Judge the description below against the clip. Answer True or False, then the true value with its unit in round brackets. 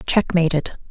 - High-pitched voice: False (170 Hz)